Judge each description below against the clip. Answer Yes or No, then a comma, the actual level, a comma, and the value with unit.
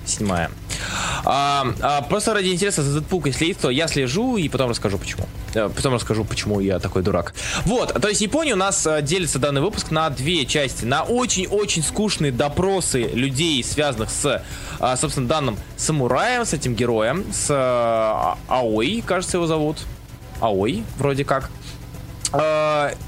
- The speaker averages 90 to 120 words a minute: No, average, 155 wpm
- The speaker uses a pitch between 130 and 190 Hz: Yes, medium, 140 Hz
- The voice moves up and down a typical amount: No, wide, 6.6 semitones